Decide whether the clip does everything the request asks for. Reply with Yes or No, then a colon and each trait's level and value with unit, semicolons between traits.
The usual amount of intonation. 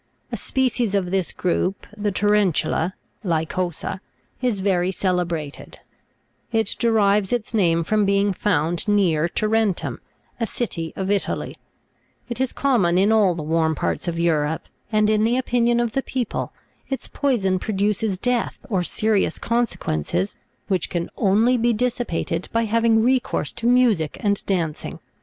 Yes: average, 4.5 semitones